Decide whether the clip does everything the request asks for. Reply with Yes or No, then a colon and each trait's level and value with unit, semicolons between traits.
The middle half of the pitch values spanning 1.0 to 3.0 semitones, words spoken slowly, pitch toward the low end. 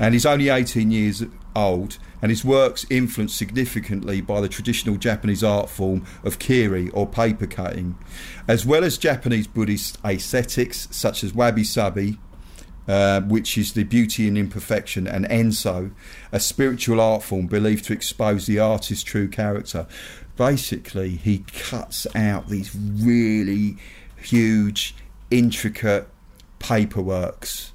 Yes: narrow, 2.6 semitones; slow, 130 wpm; low, 105 Hz